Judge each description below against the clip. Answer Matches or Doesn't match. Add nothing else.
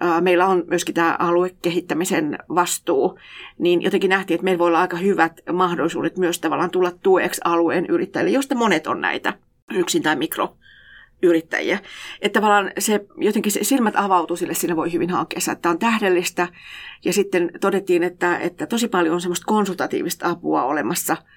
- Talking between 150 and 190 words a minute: Matches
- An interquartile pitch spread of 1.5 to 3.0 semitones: Matches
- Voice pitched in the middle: Matches